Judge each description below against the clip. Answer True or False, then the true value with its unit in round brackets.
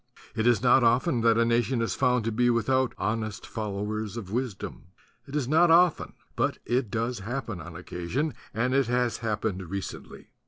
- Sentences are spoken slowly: False (185 wpm)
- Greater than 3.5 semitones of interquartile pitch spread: False (2.9 semitones)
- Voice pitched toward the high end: False (115 Hz)